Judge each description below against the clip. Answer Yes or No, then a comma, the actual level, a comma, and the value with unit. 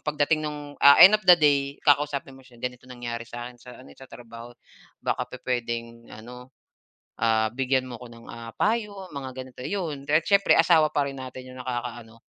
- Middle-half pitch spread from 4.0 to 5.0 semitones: No, average, 3.4 semitones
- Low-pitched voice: Yes, low, 130 Hz